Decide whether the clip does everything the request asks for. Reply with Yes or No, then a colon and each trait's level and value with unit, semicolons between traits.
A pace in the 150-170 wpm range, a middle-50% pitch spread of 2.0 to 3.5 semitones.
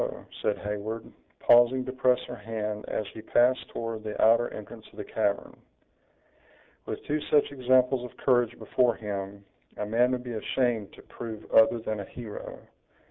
Yes: average, 165 wpm; average, 2.7 semitones